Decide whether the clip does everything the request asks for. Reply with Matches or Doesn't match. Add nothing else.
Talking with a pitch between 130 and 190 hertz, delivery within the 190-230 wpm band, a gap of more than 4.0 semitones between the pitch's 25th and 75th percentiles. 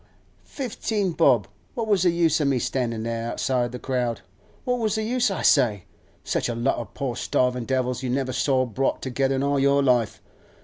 Matches